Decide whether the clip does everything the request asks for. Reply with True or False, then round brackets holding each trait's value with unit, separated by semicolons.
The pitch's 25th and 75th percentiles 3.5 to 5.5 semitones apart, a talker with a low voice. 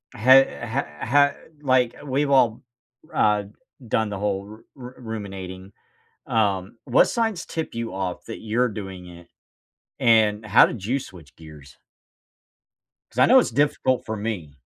True (4.7 semitones; 110 Hz)